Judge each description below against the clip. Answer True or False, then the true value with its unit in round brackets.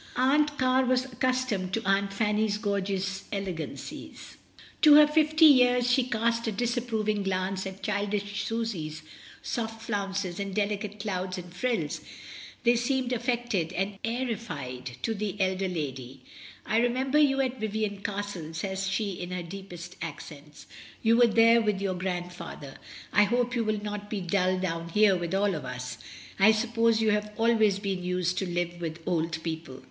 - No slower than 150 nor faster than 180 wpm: True (170 wpm)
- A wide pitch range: False (4.1 semitones)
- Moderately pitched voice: False (205 Hz)